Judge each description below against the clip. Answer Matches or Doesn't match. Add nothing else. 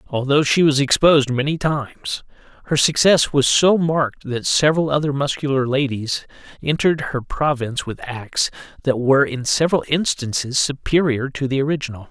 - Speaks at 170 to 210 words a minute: Doesn't match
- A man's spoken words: Matches